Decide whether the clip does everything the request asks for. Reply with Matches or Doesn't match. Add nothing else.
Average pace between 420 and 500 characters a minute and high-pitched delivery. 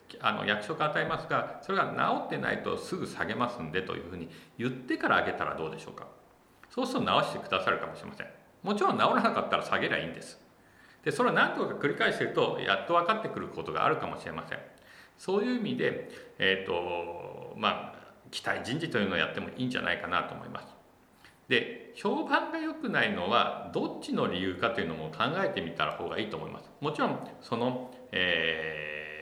Matches